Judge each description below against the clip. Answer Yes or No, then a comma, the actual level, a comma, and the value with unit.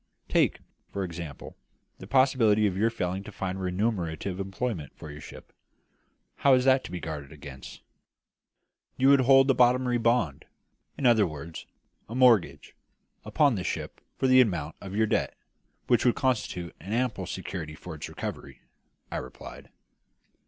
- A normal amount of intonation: No, wide, 6.5 semitones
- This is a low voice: Yes, low, 100 Hz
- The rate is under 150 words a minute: No, average, 155 wpm